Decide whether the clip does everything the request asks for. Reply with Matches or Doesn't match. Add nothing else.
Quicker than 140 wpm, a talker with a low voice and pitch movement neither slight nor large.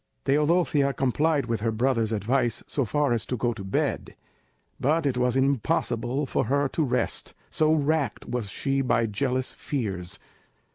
Matches